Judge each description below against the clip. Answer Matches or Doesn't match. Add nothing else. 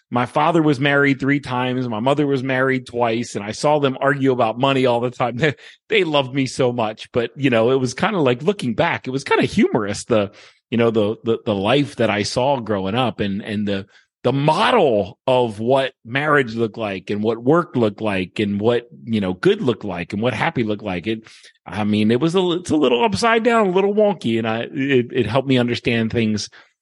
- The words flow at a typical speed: Doesn't match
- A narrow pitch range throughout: Doesn't match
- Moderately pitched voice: Doesn't match